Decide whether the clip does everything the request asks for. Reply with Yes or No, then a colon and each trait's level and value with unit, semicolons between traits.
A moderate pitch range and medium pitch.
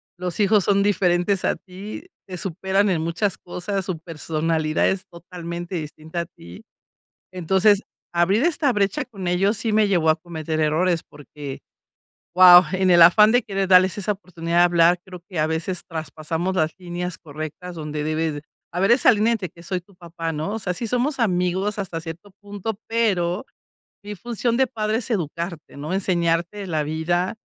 Yes: average, 3.4 semitones; medium, 180 Hz